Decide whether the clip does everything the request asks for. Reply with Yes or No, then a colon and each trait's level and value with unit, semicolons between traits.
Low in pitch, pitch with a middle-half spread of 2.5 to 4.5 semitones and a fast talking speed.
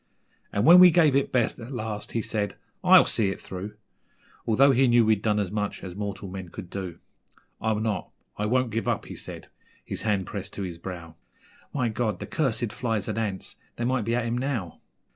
Yes: low, 110 Hz; average, 3.5 semitones; fast, 210 wpm